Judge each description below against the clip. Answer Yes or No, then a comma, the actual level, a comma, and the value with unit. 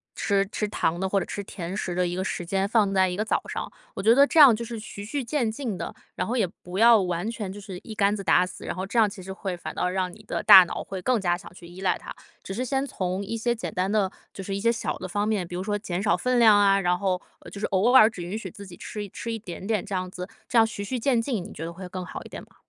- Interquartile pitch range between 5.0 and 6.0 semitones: No, average, 3.2 semitones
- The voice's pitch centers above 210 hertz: No, high, 200 Hz